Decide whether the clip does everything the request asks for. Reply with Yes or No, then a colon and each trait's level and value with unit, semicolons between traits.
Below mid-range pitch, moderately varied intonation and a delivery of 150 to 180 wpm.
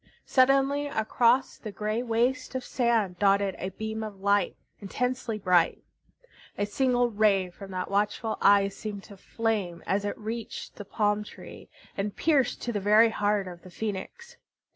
No: high, 210 Hz; average, 3.1 semitones; average, 160 wpm